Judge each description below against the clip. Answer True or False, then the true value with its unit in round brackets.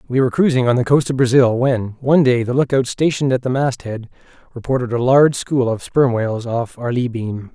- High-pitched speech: False (125 Hz)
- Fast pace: True (225 wpm)